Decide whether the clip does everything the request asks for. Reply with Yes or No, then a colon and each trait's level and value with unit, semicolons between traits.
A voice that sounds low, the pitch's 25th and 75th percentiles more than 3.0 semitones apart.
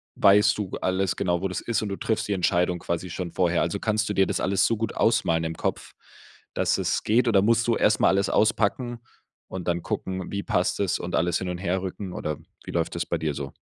Yes: very low, 95 Hz; average, 3.4 semitones